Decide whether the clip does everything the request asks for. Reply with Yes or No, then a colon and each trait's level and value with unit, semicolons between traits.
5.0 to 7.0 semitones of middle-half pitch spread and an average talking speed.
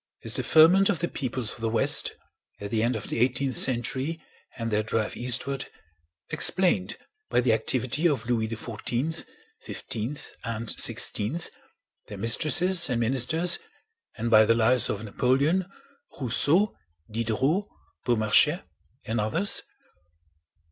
No: average, 5.3 semitones; slow, 130 wpm